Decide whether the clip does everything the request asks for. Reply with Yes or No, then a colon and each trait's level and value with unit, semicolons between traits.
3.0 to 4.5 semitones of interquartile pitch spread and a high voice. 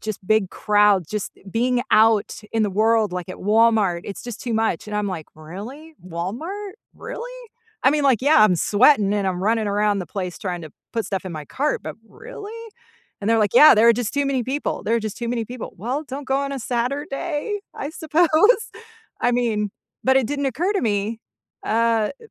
No: average, 5.2 semitones; high, 225 Hz